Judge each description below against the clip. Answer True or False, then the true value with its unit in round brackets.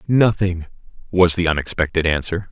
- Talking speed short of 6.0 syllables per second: True (5.2 syllables/s)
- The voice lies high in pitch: False (90 Hz)